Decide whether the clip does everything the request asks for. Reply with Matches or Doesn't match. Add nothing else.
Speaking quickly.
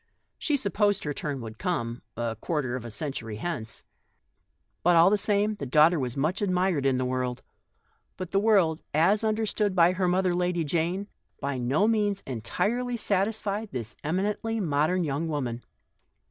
Doesn't match